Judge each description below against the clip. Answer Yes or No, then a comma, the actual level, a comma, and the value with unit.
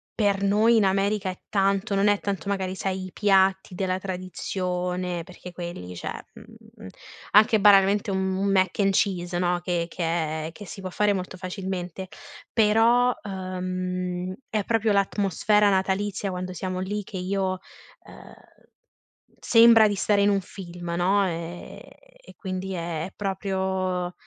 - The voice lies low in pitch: No, high, 190 Hz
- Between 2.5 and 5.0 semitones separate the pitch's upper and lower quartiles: No, narrow, 1.8 semitones